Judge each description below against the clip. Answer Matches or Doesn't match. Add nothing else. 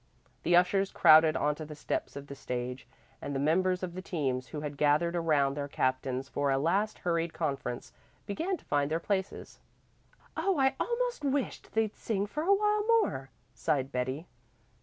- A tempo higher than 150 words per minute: Matches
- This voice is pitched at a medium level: Matches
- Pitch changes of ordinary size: Doesn't match